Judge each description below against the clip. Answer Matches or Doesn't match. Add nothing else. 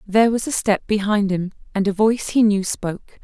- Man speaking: Doesn't match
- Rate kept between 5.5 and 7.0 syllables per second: Matches